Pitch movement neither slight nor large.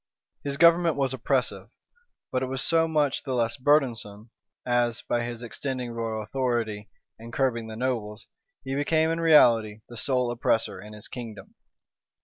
Yes: average, 3.3 semitones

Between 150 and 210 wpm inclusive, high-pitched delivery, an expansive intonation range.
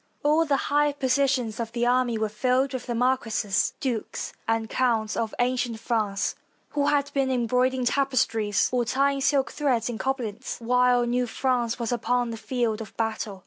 No: average, 170 wpm; high, 245 Hz; average, 2.7 semitones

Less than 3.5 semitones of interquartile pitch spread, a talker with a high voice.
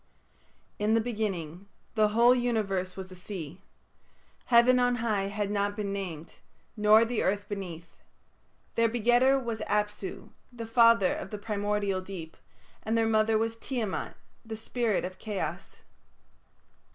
Yes: average, 2.9 semitones; high, 210 Hz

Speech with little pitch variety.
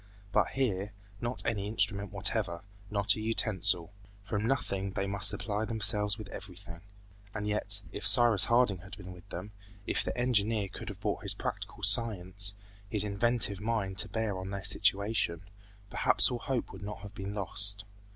Yes: narrow, 2.0 semitones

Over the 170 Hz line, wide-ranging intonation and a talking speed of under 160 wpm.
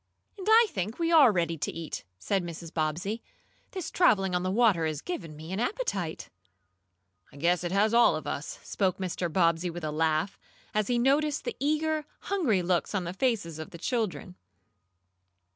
No: high, 190 Hz; wide, 6.7 semitones; average, 180 wpm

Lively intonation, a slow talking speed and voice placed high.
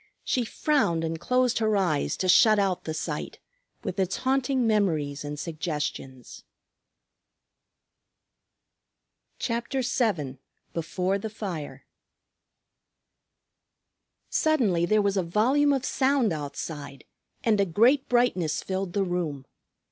Yes: wide, 6.7 semitones; slow, 110 wpm; high, 195 Hz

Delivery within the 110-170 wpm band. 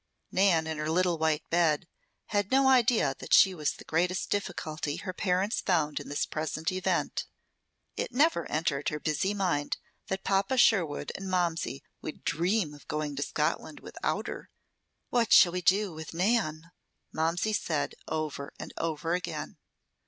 Yes: average, 160 wpm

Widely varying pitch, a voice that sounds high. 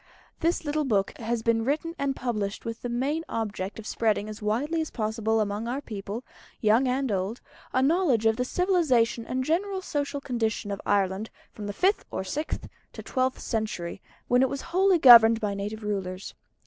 No: average, 4.9 semitones; high, 230 Hz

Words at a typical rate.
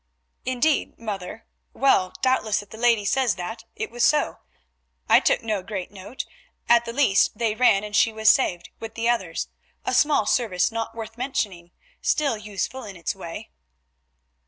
Yes: average, 165 wpm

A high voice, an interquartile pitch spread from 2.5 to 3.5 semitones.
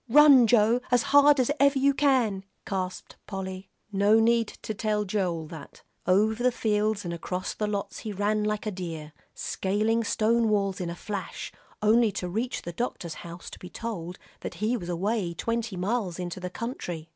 No: high, 210 Hz; average, 4.0 semitones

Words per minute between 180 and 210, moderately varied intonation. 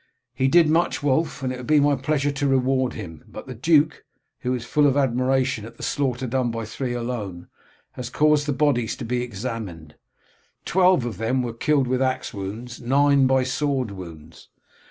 Yes: average, 190 wpm; average, 3.5 semitones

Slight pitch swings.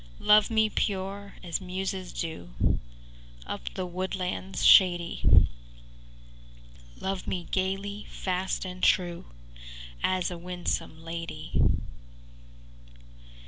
Yes: narrow, 1.8 semitones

